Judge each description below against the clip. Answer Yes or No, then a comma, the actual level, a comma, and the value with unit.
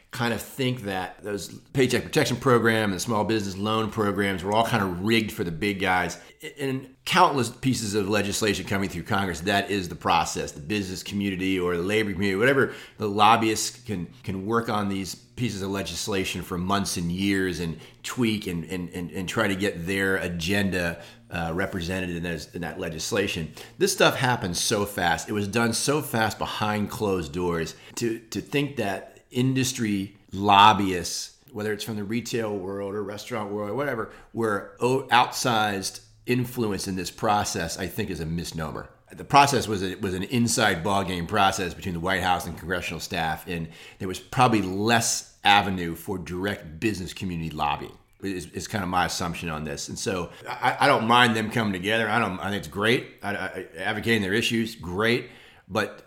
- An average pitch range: Yes, average, 3.6 semitones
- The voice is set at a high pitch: No, low, 100 Hz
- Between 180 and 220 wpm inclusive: Yes, average, 185 wpm